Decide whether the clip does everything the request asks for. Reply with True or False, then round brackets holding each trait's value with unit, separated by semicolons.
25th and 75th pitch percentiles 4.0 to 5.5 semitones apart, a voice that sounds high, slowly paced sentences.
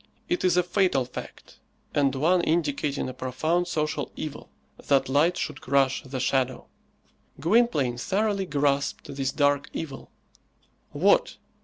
False (4.5 semitones; 145 Hz; 130 wpm)